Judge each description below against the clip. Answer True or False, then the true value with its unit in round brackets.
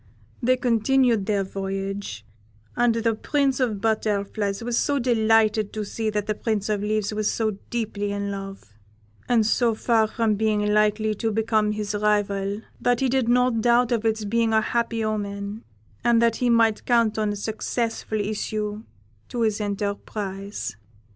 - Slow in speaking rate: False (165 wpm)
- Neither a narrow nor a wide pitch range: False (2.0 semitones)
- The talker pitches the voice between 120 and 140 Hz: False (215 Hz)